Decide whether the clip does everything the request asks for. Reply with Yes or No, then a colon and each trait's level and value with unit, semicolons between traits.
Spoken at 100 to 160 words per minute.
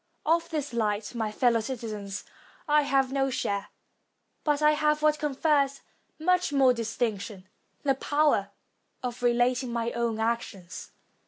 Yes: slow, 135 wpm